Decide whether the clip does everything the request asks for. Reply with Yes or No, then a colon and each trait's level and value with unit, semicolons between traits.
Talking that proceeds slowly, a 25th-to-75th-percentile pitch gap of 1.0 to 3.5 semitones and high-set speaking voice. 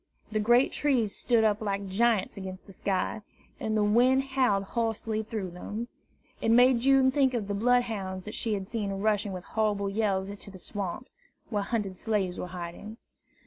No: average, 180 wpm; average, 3.1 semitones; high, 210 Hz